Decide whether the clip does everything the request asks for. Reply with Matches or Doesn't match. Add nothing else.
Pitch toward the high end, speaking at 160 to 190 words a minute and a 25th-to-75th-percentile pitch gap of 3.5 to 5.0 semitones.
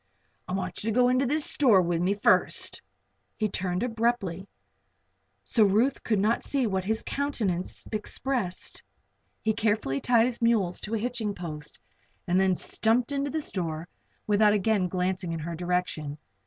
Matches